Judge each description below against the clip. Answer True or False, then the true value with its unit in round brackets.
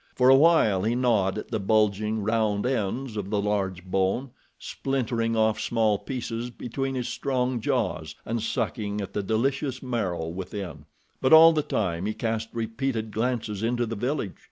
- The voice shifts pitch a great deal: False (3.6 semitones)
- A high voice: False (110 Hz)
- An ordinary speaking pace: True (160 wpm)